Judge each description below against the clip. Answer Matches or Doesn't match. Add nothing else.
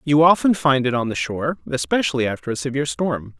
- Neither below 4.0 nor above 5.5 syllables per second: Doesn't match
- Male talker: Matches